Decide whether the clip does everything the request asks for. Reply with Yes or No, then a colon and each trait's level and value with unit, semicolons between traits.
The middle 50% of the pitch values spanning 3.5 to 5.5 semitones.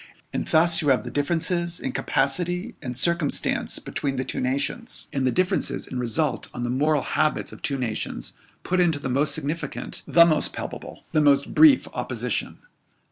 Yes: average, 4.3 semitones